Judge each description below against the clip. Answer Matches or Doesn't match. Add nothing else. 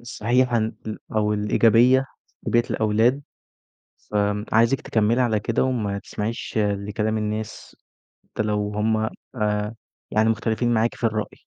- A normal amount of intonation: Doesn't match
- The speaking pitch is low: Matches